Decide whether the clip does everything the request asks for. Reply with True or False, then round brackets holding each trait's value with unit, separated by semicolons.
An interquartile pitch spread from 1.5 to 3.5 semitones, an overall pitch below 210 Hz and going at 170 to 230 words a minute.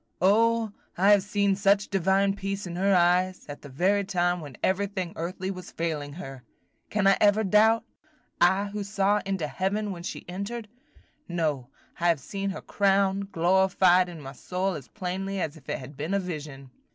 True (2.7 semitones; 190 Hz; 180 wpm)